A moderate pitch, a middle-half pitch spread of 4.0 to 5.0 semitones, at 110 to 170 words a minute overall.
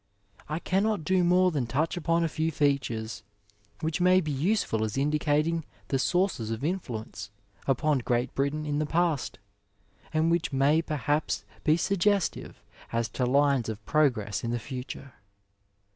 Yes: medium, 150 Hz; average, 4.7 semitones; average, 150 wpm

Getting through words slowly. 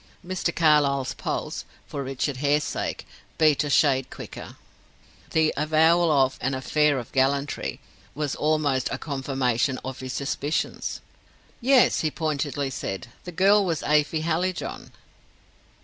Yes: slow, 130 wpm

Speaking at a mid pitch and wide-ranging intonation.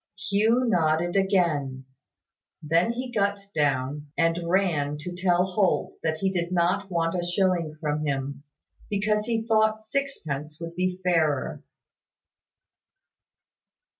No: medium, 175 Hz; average, 4.4 semitones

